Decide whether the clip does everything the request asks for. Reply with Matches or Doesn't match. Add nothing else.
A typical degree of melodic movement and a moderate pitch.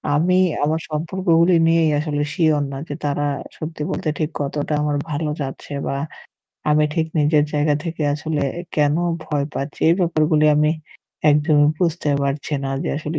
Doesn't match